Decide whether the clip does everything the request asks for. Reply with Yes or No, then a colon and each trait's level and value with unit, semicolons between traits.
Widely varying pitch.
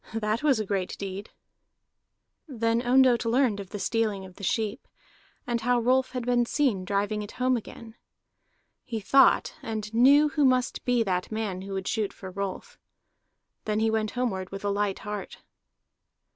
No: average, 3.7 semitones